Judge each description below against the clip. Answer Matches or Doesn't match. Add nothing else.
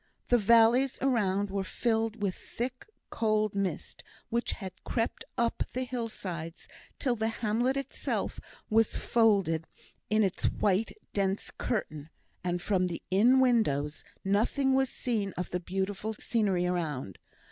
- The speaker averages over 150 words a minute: Doesn't match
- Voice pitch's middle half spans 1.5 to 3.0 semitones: Doesn't match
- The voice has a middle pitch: Doesn't match